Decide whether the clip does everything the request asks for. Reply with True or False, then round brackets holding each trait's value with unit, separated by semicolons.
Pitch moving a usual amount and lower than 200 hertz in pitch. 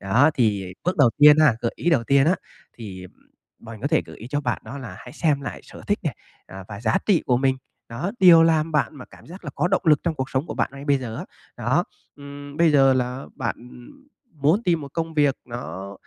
True (4.5 semitones; 140 Hz)